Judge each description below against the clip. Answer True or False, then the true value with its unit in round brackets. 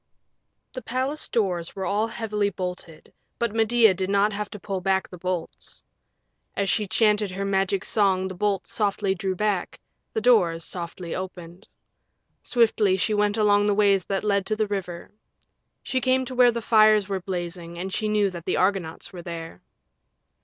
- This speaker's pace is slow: False (170 wpm)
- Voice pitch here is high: True (200 Hz)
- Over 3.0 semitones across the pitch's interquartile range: False (2.5 semitones)